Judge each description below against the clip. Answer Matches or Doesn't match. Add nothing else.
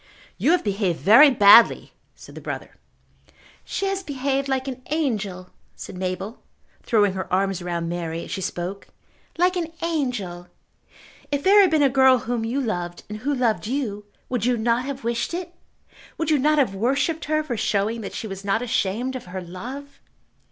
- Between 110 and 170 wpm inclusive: Doesn't match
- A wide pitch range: Matches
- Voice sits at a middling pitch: Doesn't match